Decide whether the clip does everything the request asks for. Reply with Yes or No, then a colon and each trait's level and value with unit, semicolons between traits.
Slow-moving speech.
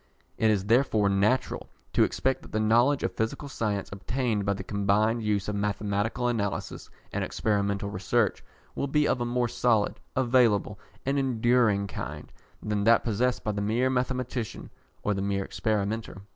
No: average, 160 wpm